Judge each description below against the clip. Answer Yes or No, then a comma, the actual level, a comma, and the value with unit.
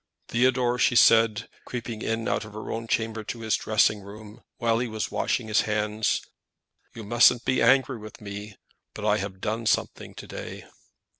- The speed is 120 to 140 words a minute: No, average, 175 wpm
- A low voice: Yes, low, 110 Hz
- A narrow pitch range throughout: Yes, narrow, 1.7 semitones